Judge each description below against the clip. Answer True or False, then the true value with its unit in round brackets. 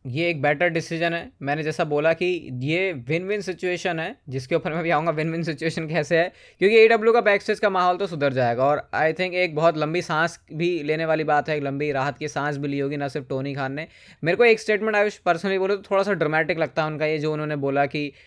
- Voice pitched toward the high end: False (165 Hz)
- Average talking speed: False (260 wpm)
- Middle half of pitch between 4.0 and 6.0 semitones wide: False (3.3 semitones)